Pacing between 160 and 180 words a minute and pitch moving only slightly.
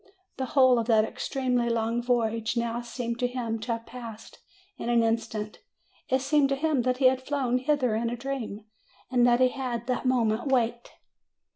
No: average, 190 wpm; narrow, 2.0 semitones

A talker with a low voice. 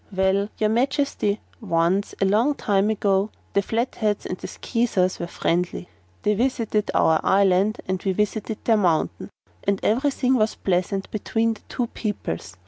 No: high, 205 Hz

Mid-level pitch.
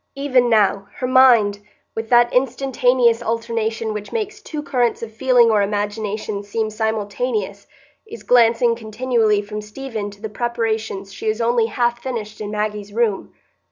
No: high, 225 Hz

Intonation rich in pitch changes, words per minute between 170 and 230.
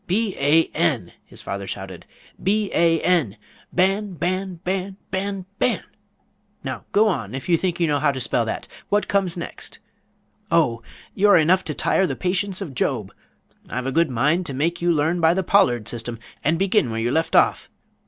Yes: wide, 6.0 semitones; average, 185 wpm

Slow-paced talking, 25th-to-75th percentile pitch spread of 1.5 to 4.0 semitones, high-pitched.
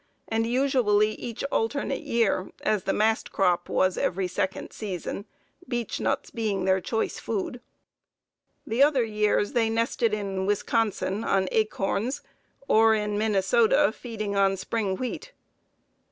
Yes: slow, 130 wpm; average, 2.8 semitones; high, 215 Hz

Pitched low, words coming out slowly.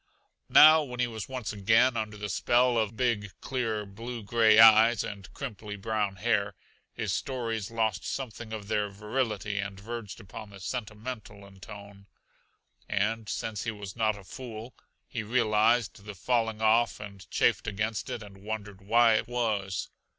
No: low, 110 Hz; average, 160 wpm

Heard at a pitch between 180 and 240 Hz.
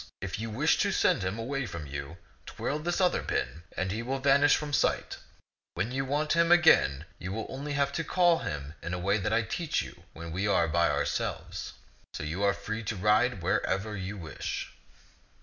No: low, 105 Hz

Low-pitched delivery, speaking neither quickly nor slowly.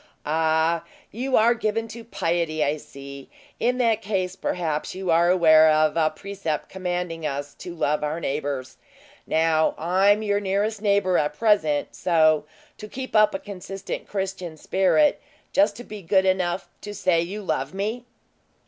No: medium, 180 Hz; average, 155 wpm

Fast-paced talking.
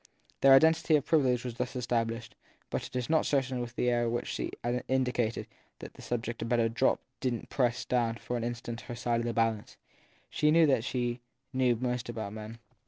Yes: fast, 210 wpm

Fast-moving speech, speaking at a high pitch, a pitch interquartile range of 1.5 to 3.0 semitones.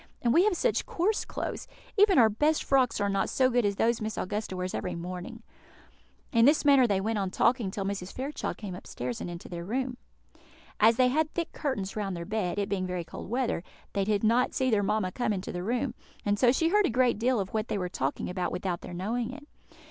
No: fast, 230 wpm; high, 215 Hz; average, 5.3 semitones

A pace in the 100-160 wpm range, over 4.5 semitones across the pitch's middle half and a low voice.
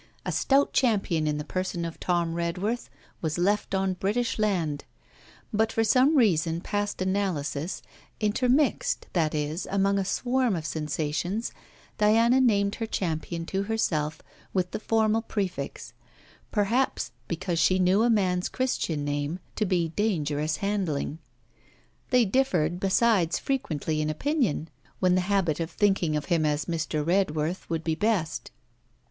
No: average, 140 wpm; average, 5.0 semitones; medium, 185 Hz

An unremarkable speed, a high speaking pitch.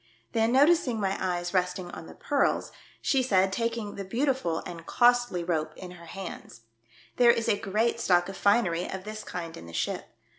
Yes: average, 190 wpm; high, 195 Hz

